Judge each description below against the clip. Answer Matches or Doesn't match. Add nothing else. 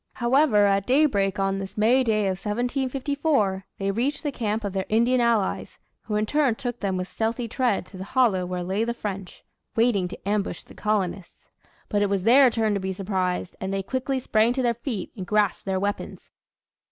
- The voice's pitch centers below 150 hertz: Doesn't match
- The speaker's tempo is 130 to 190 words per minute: Doesn't match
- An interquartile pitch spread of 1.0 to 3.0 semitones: Doesn't match